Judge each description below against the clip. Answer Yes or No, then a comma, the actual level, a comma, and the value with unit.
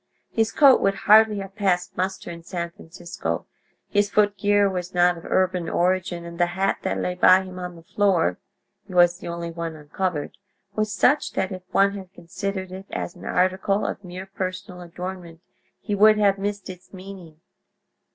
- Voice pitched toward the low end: No, medium, 185 Hz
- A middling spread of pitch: No, narrow, 2.2 semitones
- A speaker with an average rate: Yes, average, 180 wpm